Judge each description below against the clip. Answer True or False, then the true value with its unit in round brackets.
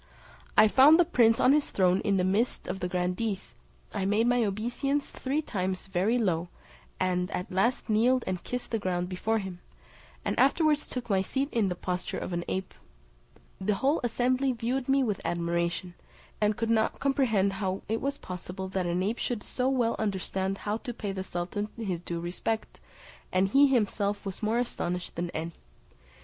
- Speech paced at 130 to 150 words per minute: False (185 wpm)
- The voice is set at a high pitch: True (205 Hz)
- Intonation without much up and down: False (4.8 semitones)